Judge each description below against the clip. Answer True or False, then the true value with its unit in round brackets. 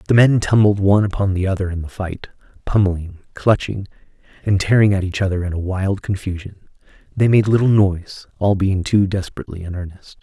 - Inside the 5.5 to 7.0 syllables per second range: True (6.0 syllables/s)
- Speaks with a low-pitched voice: True (95 Hz)